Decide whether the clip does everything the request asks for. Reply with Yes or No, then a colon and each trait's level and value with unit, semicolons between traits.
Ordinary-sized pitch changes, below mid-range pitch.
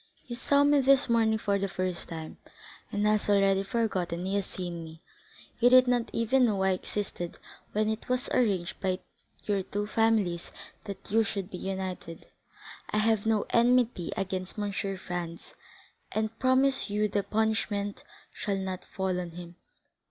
No: average, 3.3 semitones; high, 205 Hz